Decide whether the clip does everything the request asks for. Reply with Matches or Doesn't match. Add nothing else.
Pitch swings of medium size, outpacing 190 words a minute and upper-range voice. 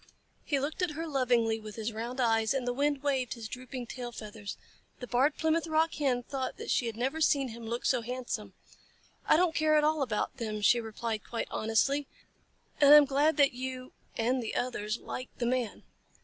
Matches